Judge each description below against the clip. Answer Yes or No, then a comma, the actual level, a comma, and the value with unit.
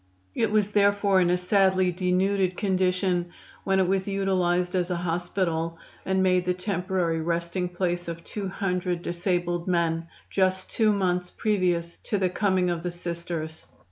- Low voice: No, medium, 180 Hz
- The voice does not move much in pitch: Yes, narrow, 1.6 semitones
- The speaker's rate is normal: Yes, average, 155 wpm